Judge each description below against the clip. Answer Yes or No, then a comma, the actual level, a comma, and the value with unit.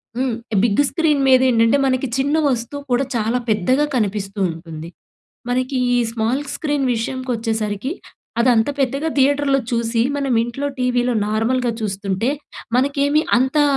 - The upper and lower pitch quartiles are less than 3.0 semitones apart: No, average, 3.5 semitones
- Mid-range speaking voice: No, very high, 250 Hz